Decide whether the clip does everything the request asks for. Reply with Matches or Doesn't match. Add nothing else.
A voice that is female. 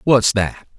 Doesn't match